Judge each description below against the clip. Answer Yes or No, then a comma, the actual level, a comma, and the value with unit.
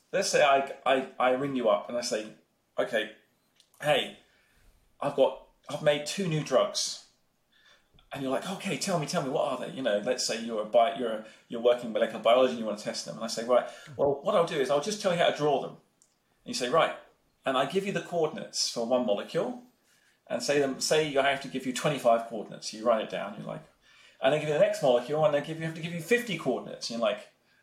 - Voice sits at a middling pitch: Yes, medium, 145 Hz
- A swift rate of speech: Yes, fast, 255 wpm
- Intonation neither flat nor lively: Yes, average, 4.1 semitones